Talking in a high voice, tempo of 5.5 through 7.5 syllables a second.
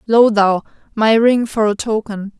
No: high, 215 Hz; 4.2 syllables/s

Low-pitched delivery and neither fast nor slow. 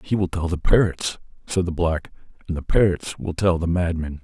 No: very low, 85 Hz; fast, 210 wpm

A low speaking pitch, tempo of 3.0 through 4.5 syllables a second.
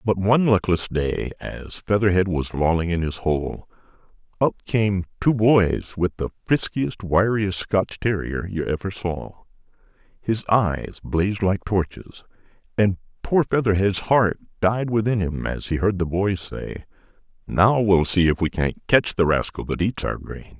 Yes: very low, 95 Hz; 4.2 syllables/s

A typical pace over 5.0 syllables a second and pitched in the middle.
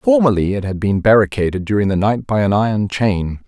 No: 5.6 syllables/s; low, 105 Hz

